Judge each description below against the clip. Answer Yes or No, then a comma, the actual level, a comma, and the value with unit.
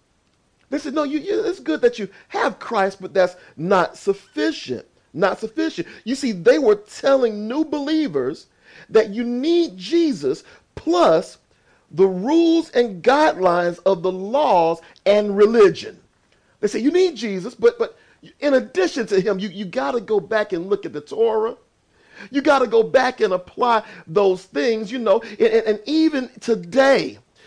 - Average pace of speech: Yes, average, 165 wpm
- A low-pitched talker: No, high, 245 Hz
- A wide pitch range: Yes, wide, 7.6 semitones